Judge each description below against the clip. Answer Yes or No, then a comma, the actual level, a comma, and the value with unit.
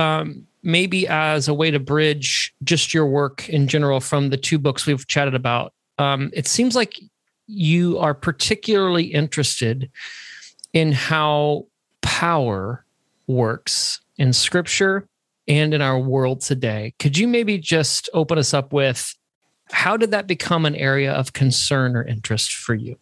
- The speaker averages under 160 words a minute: Yes, average, 150 wpm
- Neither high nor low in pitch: Yes, medium, 145 Hz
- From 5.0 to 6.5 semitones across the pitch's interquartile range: No, average, 4.0 semitones